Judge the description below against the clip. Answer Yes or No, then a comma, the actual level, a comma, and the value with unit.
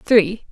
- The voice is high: Yes, high, 210 Hz